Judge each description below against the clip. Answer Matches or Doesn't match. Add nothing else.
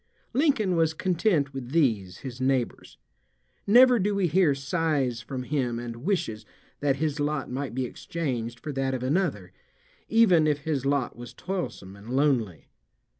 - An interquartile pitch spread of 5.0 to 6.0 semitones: Matches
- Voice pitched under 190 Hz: Matches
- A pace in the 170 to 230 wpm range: Doesn't match